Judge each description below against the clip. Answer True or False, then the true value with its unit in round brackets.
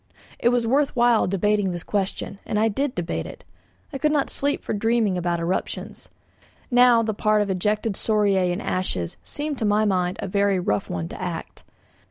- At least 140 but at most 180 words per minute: False (190 wpm)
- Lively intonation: False (4.1 semitones)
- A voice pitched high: True (210 Hz)